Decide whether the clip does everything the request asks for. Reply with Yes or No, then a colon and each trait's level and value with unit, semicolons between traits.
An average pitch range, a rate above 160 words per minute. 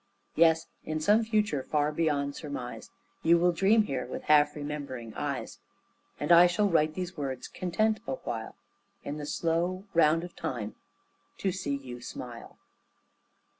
No: average, 3.9 semitones; average, 145 wpm